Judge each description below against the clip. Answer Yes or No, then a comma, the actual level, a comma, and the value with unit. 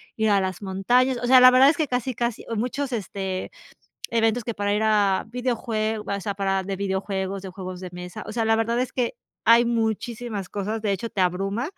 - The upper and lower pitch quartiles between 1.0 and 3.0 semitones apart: No, average, 3.5 semitones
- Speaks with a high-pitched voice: Yes, high, 215 Hz